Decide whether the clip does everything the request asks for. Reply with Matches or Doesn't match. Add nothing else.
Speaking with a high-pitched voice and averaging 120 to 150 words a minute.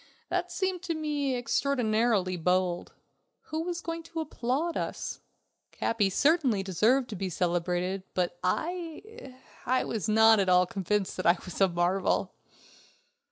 Matches